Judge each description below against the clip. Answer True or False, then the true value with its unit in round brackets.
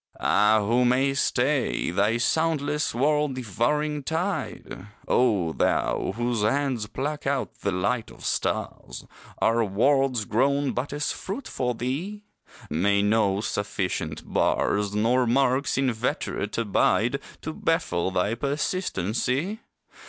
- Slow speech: True (115 wpm)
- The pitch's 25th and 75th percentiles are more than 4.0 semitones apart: True (5.2 semitones)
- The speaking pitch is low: True (125 Hz)